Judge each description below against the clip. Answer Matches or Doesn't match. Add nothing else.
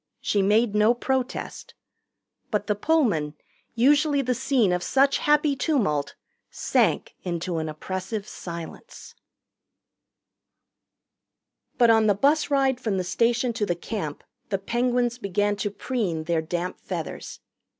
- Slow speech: Matches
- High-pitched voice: Matches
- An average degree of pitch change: Doesn't match